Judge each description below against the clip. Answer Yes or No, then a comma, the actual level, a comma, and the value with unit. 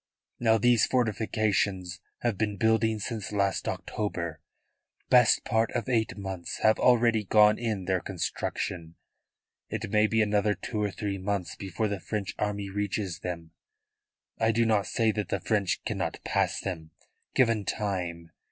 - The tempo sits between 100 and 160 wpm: Yes, average, 150 wpm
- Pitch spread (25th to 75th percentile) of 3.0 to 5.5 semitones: No, narrow, 2.6 semitones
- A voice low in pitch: Yes, low, 105 Hz